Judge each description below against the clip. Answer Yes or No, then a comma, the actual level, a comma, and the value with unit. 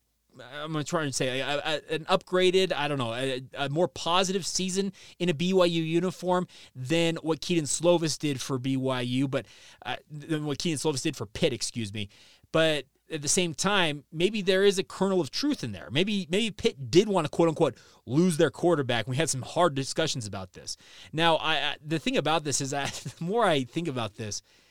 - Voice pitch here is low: No, medium, 160 Hz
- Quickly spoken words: Yes, fast, 210 wpm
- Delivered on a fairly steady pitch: No, average, 4.7 semitones